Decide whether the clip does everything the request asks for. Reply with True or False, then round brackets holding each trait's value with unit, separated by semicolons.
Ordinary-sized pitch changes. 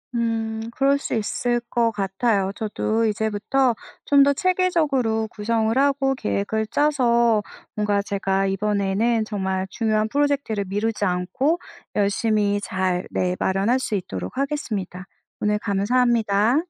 True (3.5 semitones)